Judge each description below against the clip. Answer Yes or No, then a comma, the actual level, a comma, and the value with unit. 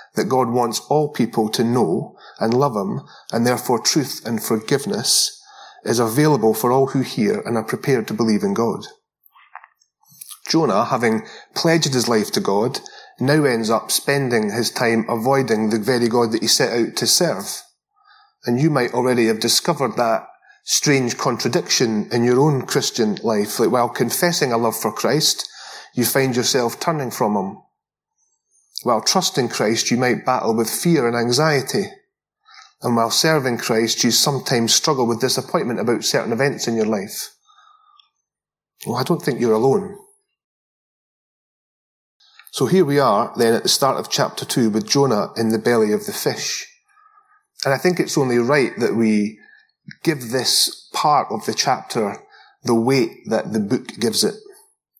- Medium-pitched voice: No, low, 130 Hz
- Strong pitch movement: Yes, wide, 7.8 semitones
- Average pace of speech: Yes, average, 165 wpm